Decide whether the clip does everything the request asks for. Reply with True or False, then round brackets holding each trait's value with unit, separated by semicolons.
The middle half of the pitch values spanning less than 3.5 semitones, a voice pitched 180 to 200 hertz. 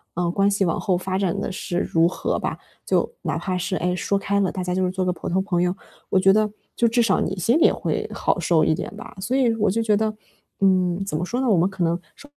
True (2.7 semitones; 190 Hz)